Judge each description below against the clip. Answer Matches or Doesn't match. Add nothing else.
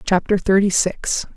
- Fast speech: Doesn't match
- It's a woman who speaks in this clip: Matches